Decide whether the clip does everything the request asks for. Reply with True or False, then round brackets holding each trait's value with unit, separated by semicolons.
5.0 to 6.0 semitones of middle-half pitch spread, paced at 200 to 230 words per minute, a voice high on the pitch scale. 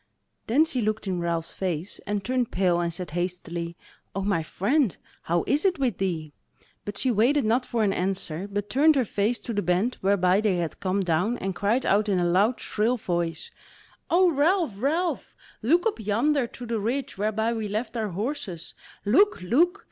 False (5.6 semitones; 190 wpm; 210 Hz)